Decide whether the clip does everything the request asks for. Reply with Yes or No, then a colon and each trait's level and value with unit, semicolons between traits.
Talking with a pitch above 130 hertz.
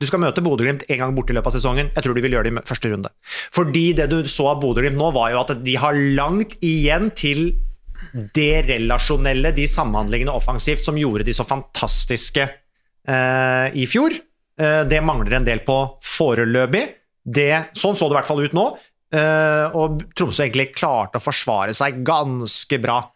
Yes: medium, 140 Hz